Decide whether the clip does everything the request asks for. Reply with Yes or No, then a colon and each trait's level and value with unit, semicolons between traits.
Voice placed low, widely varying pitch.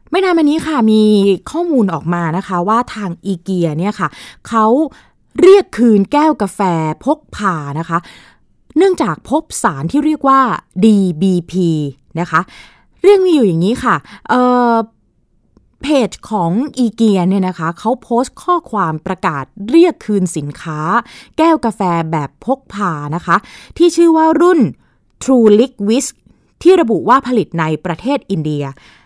No: high, 215 Hz; wide, 7.7 semitones